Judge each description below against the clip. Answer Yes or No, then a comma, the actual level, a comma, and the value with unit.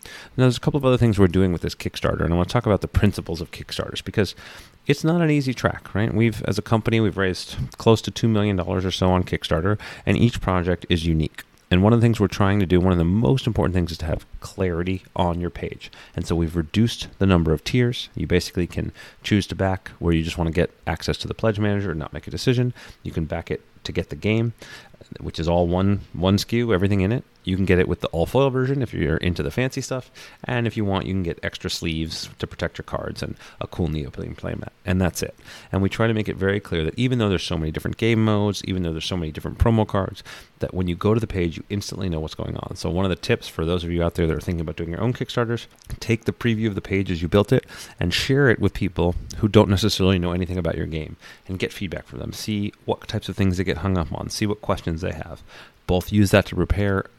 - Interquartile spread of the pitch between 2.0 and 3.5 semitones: No, average, 4.3 semitones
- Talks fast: Yes, fast, 275 wpm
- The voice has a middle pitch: No, very low, 95 Hz